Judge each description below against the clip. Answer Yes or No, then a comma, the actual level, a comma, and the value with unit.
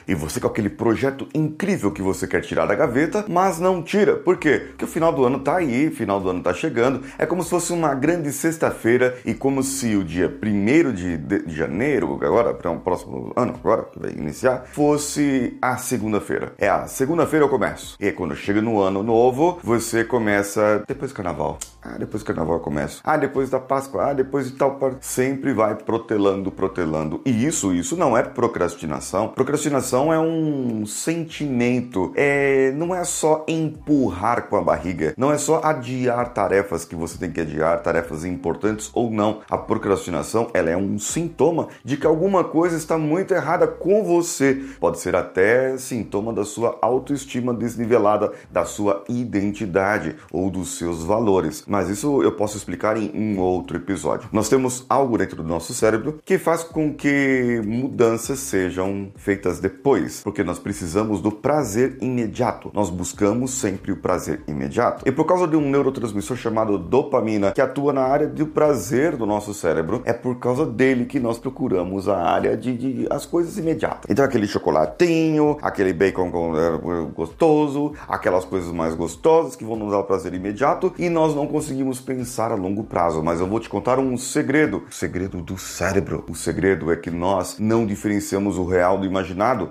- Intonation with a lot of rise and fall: Yes, wide, 6.6 semitones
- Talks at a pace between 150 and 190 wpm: Yes, average, 180 wpm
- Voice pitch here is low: Yes, low, 120 Hz